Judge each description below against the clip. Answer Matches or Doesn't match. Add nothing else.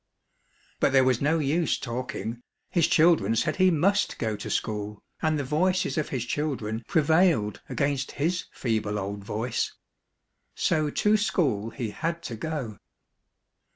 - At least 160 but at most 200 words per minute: Doesn't match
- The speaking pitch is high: Doesn't match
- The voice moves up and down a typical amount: Doesn't match